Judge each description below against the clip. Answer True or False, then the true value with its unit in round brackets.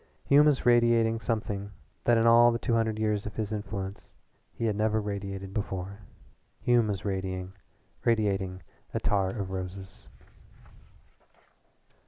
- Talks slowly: True (125 wpm)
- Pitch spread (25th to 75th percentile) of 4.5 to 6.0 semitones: False (2.9 semitones)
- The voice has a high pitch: False (105 Hz)